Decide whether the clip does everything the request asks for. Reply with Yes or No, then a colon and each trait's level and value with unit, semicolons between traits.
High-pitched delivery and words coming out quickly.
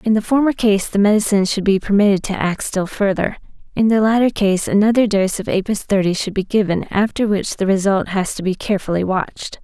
Yes: high, 200 Hz; fast, 210 wpm